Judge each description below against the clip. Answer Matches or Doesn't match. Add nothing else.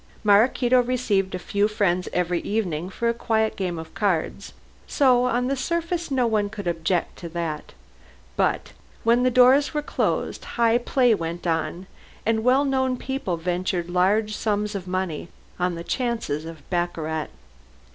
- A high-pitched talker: Matches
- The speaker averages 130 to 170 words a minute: Matches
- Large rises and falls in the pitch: Matches